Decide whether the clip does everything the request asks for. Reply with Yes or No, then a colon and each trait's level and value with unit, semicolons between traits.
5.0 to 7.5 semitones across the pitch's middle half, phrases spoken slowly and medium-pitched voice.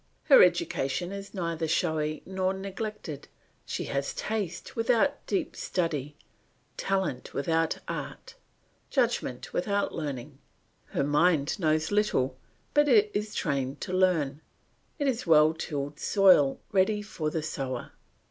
Yes: wide, 5.6 semitones; slow, 125 wpm; medium, 170 Hz